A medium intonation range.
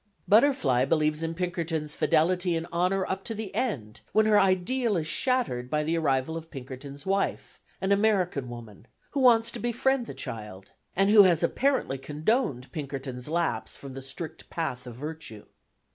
No: wide, 6.7 semitones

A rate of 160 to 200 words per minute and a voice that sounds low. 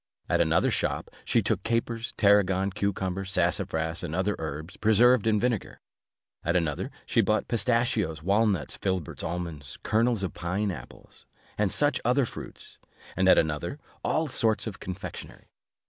No: average, 145 wpm; low, 100 Hz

